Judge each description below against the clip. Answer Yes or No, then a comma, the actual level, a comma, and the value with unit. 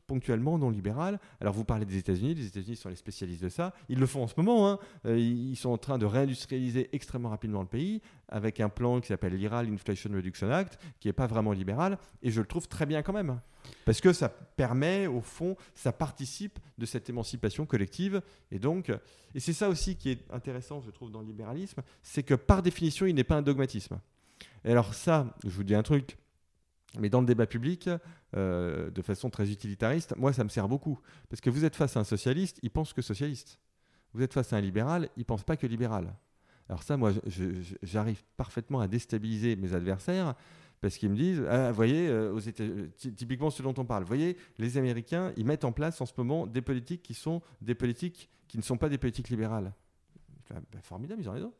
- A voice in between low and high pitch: No, low, 125 Hz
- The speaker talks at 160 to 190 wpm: No, fast, 220 wpm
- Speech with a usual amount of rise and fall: No, wide, 5.9 semitones